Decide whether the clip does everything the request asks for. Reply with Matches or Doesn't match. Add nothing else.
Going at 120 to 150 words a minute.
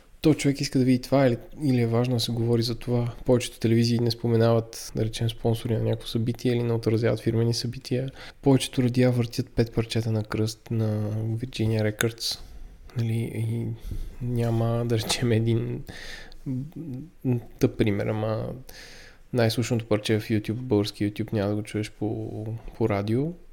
Doesn't match